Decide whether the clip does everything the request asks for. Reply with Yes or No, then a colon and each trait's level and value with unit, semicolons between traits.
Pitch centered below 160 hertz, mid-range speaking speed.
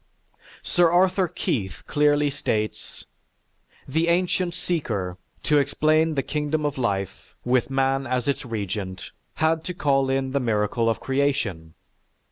No: low, 135 Hz; slow, 130 wpm